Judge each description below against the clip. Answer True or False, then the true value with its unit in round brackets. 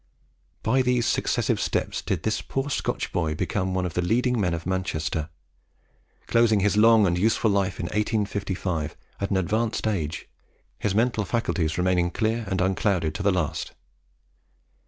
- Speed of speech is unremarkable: True (155 wpm)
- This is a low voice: True (100 Hz)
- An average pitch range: True (3.9 semitones)